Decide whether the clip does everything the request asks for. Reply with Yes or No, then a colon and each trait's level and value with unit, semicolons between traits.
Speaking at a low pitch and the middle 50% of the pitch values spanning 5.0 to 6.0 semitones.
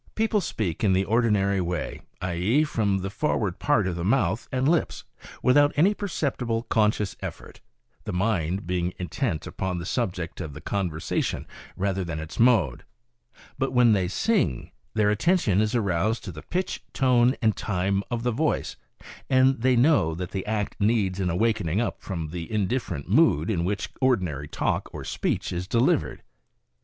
Yes: low, 105 Hz; average, 5.3 semitones